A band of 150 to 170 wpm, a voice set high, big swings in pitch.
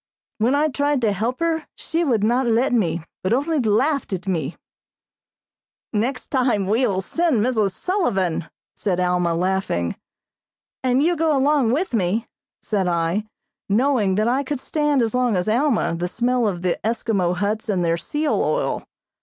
Yes: average, 165 wpm; high, 225 Hz; wide, 6.4 semitones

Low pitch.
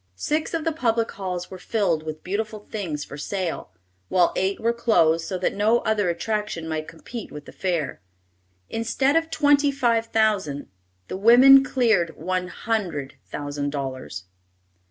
No: high, 195 Hz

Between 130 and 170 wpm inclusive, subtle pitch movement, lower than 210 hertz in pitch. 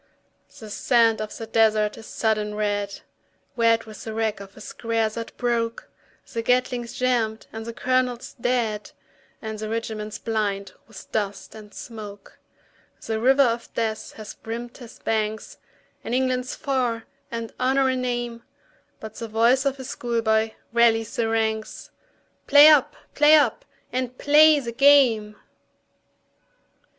No: average, 140 wpm; narrow, 2.3 semitones; high, 230 Hz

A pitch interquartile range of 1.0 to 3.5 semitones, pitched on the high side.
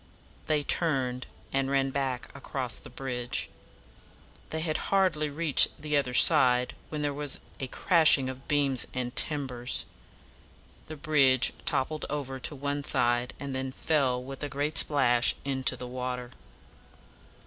No: narrow, 2.6 semitones; low, 135 Hz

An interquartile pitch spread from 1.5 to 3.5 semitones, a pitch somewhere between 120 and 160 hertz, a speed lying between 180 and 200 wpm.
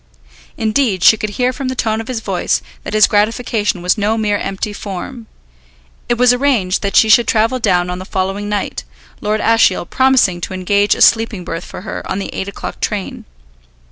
No: average, 3.0 semitones; high, 210 Hz; average, 195 wpm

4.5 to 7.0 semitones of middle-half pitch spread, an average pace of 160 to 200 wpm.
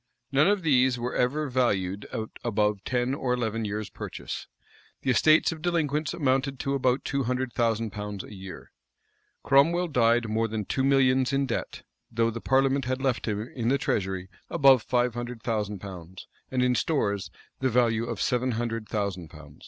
No: average, 3.8 semitones; average, 180 wpm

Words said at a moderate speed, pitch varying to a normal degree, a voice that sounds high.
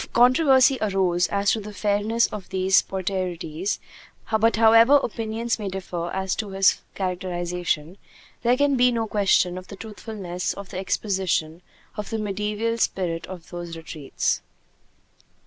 Yes: average, 145 wpm; average, 3.7 semitones; high, 195 Hz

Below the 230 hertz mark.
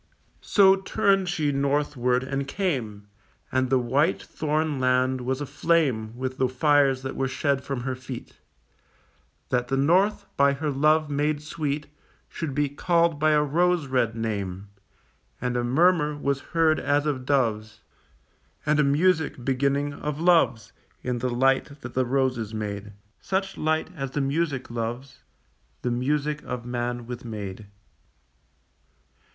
Yes: low, 135 Hz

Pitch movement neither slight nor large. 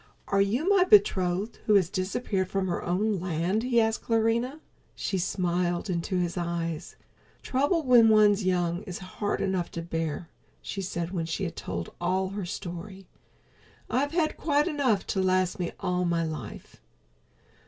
Yes: average, 4.1 semitones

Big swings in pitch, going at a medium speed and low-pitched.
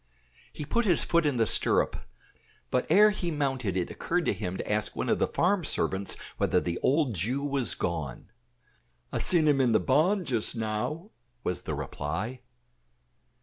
Yes: wide, 7.8 semitones; average, 175 wpm; low, 130 Hz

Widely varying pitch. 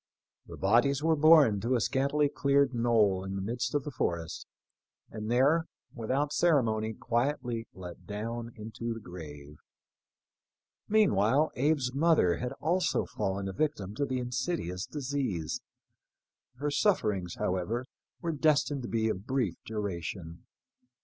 Yes: wide, 5.9 semitones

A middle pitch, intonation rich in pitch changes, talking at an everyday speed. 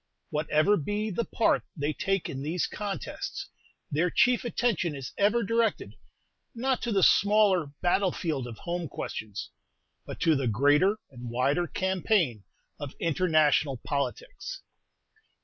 No: medium, 175 Hz; wide, 6.3 semitones; slow, 130 wpm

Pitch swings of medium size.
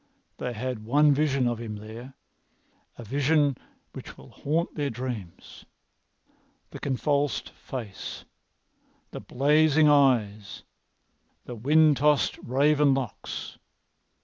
Yes: average, 3.8 semitones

